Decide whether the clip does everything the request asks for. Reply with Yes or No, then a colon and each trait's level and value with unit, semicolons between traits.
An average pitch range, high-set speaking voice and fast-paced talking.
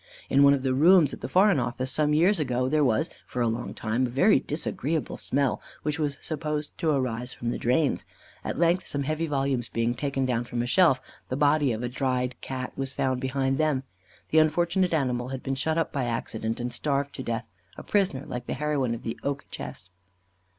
No: average, 3.6 semitones; low, 135 Hz; fast, 215 wpm